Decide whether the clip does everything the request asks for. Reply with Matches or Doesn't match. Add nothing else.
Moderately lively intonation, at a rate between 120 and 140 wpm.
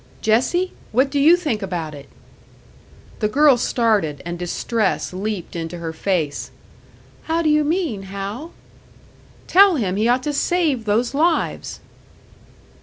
Doesn't match